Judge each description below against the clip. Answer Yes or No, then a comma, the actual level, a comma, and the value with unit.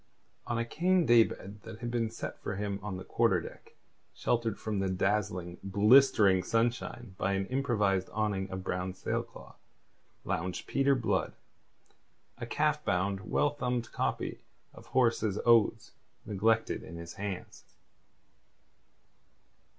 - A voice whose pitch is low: Yes, low, 105 Hz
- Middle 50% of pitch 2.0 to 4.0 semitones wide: Yes, average, 3.5 semitones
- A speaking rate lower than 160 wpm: Yes, slow, 135 wpm